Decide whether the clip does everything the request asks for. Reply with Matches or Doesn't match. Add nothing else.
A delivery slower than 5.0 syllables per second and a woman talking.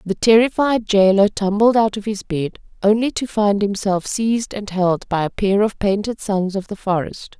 Matches